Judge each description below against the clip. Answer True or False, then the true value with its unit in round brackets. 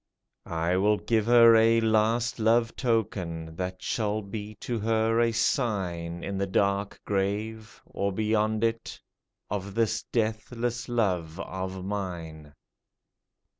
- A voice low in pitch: True (105 Hz)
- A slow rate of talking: True (130 wpm)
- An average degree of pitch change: True (3.1 semitones)